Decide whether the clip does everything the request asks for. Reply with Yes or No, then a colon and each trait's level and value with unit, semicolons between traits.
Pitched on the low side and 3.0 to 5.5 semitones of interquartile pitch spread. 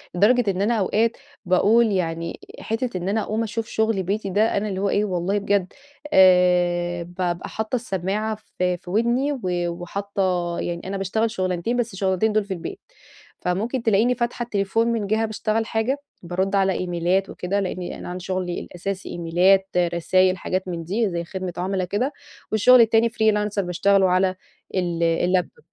No: high, 195 Hz; average, 3.4 semitones